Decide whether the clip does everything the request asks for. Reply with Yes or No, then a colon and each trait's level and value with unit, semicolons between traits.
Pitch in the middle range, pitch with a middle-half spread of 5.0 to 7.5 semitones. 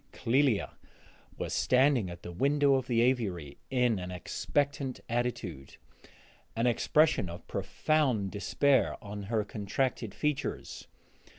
No: low, 120 Hz; average, 5.3 semitones